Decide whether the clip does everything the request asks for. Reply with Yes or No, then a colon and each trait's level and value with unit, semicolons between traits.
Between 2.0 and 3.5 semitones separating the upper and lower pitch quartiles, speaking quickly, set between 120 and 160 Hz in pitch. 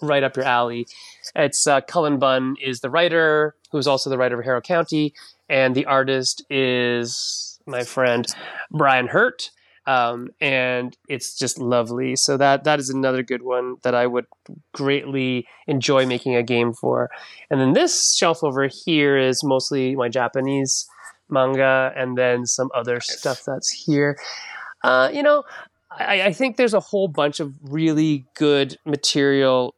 No: average, 3.0 semitones; average, 160 wpm; low, 135 Hz